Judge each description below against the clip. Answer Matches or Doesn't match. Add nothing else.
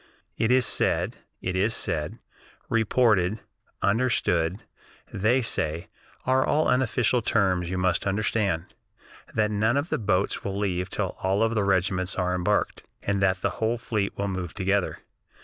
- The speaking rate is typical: Matches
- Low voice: Matches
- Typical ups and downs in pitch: Matches